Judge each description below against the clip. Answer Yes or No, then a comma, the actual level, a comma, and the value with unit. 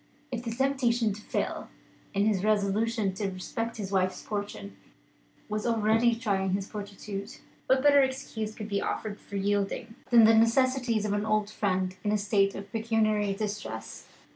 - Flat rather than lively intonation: Yes, narrow, 2.3 semitones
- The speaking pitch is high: Yes, high, 210 Hz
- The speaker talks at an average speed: Yes, average, 165 wpm